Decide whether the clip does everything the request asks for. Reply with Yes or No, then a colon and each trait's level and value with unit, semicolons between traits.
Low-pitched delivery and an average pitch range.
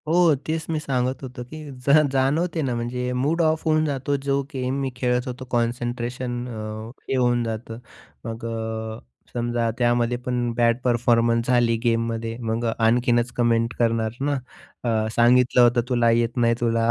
No: low, 120 Hz; narrow, 1.8 semitones